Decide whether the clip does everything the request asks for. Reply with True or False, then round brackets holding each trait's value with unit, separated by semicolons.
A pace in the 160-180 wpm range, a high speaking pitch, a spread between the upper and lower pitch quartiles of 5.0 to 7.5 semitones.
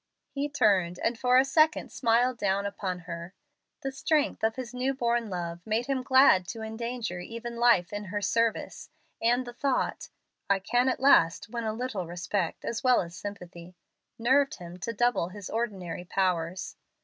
True (175 wpm; 225 Hz; 5.3 semitones)